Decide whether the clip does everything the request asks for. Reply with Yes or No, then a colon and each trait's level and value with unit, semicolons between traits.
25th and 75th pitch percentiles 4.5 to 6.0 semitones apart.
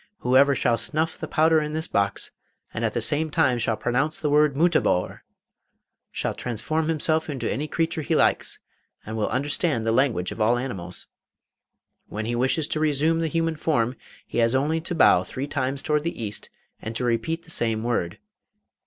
Yes: average, 5.2 semitones